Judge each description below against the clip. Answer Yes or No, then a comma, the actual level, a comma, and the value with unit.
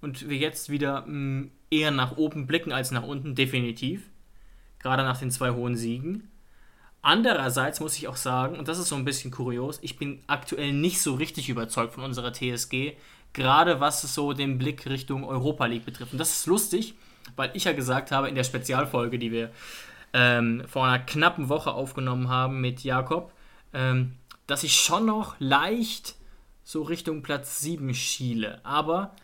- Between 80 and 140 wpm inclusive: No, average, 170 wpm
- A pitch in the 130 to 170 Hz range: Yes, medium, 140 Hz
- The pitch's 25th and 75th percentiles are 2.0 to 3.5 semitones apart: Yes, average, 3.2 semitones